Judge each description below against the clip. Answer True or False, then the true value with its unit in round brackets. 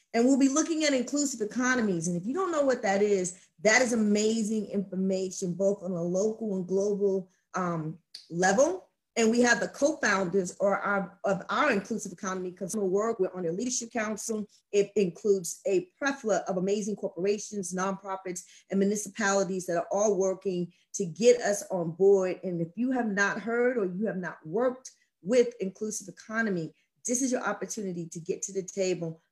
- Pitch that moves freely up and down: False (3.1 semitones)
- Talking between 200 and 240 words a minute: False (175 wpm)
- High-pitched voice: True (200 Hz)